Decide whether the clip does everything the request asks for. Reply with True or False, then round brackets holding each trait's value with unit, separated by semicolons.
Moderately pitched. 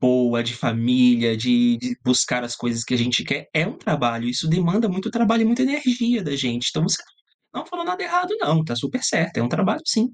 True (160 Hz)